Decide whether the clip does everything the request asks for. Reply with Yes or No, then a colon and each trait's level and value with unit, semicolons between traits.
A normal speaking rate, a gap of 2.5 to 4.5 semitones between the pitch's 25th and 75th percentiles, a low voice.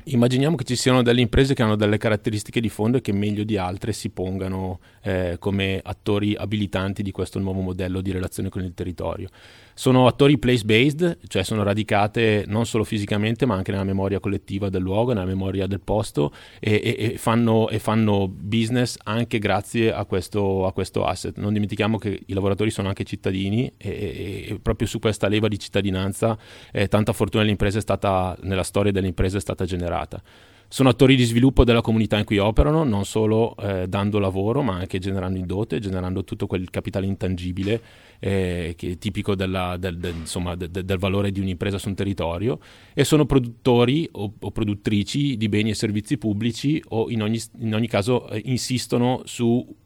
No: fast, 185 wpm; average, 2.9 semitones; low, 105 Hz